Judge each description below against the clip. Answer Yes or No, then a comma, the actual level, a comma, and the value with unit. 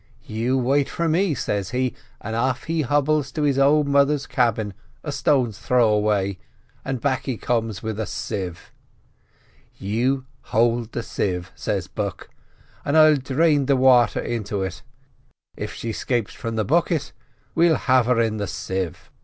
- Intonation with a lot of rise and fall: No, average, 4.4 semitones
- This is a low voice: Yes, low, 125 Hz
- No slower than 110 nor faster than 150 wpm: No, average, 160 wpm